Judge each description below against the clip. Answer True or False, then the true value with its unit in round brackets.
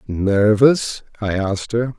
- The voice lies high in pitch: False (110 Hz)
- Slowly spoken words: True (120 wpm)